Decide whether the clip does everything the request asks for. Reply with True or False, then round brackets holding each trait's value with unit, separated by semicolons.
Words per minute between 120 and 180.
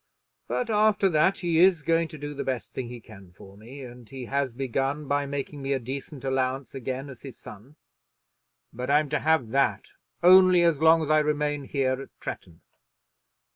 False (190 wpm)